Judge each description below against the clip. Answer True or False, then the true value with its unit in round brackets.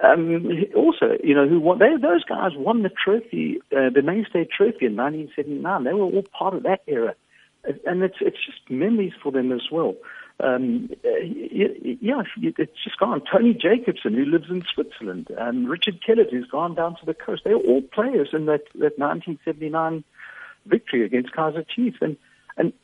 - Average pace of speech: True (195 wpm)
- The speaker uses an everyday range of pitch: False (7.4 semitones)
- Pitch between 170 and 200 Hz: True (185 Hz)